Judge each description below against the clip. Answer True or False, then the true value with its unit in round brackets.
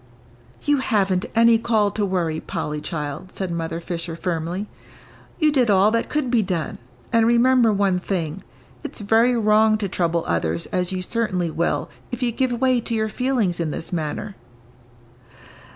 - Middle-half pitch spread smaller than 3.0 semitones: False (5.2 semitones)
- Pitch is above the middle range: True (200 Hz)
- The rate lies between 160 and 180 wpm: True (165 wpm)